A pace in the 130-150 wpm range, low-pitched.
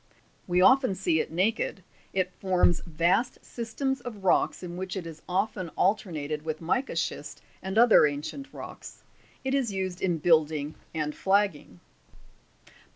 No: average, 145 wpm; medium, 185 Hz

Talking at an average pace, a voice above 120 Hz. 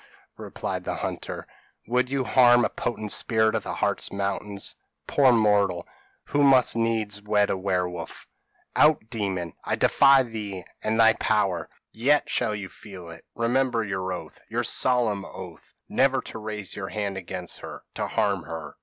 No: average, 160 wpm; low, 105 Hz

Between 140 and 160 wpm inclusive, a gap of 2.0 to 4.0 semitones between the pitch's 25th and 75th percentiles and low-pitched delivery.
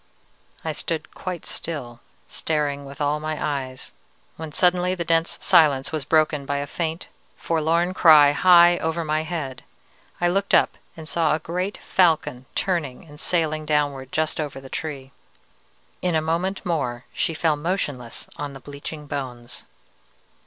No: average, 150 wpm; average, 3.0 semitones; medium, 155 Hz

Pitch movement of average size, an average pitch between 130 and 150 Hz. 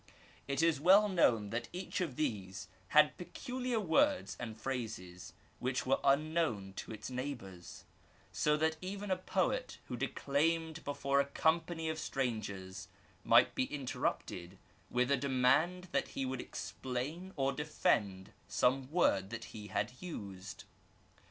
No: wide, 6.7 semitones; low, 135 Hz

